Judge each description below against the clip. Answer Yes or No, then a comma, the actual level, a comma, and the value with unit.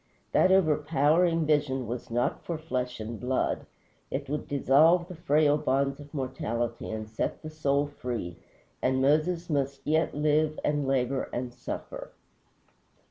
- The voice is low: No, medium, 145 Hz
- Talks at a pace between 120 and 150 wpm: Yes, average, 140 wpm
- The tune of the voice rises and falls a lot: No, average, 3.3 semitones